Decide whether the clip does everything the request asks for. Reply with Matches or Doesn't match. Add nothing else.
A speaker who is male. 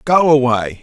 Matches